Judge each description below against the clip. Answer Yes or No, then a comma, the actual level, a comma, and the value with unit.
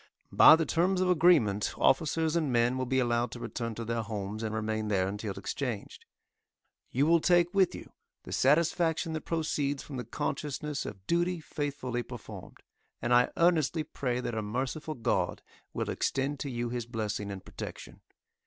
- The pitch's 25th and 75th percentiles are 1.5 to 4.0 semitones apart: No, wide, 5.5 semitones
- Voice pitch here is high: No, low, 130 Hz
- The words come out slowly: No, average, 170 wpm